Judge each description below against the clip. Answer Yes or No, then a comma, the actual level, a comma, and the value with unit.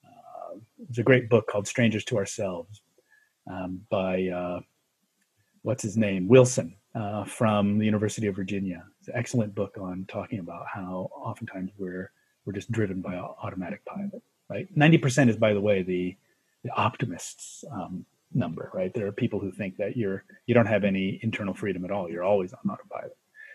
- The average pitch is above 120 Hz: No, low, 105 Hz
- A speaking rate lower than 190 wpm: Yes, average, 180 wpm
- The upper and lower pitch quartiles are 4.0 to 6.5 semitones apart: Yes, average, 4.3 semitones